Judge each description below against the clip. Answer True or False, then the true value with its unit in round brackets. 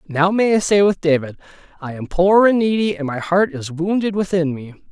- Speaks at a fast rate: True (220 wpm)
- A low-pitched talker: False (175 Hz)